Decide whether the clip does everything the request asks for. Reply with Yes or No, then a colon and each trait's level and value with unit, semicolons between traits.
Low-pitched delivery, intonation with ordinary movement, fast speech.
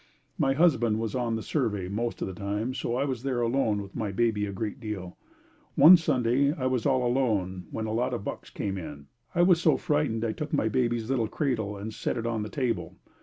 Yes: low, 115 Hz; average, 3.7 semitones; fast, 225 wpm